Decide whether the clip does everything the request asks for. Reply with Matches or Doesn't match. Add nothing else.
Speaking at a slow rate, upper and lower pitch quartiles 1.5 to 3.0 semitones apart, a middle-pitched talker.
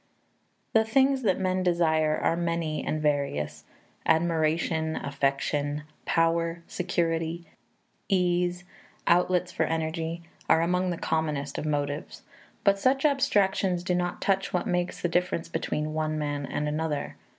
Matches